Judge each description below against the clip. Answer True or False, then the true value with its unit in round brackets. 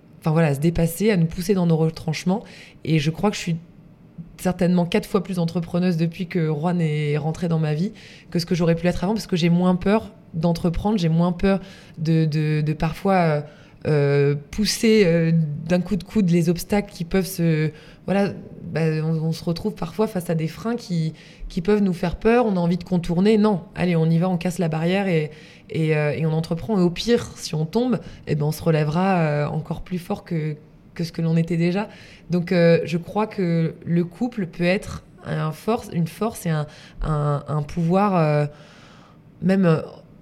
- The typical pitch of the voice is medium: True (170 Hz)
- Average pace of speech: True (210 wpm)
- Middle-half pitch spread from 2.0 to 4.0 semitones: True (2.8 semitones)